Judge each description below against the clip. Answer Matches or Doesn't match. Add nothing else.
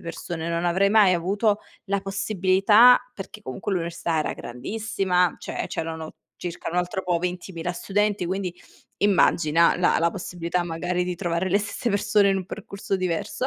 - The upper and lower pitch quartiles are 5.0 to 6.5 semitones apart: Doesn't match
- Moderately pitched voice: Matches